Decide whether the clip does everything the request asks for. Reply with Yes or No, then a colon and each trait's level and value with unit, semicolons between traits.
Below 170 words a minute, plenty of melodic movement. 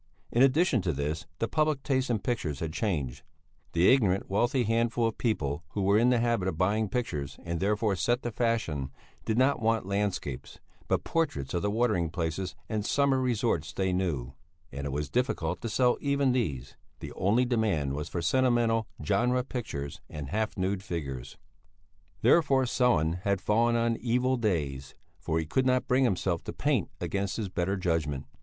No: average, 175 wpm; wide, 6.7 semitones